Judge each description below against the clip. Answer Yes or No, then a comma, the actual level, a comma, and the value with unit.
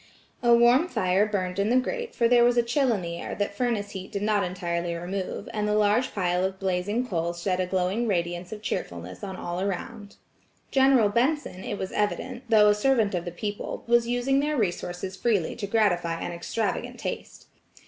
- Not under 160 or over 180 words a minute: No, average, 200 wpm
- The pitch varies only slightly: No, average, 4.6 semitones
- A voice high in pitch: Yes, high, 205 Hz